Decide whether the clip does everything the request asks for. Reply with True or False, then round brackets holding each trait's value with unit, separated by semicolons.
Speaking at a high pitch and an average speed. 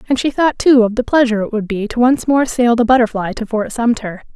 False (235 Hz; 260 wpm)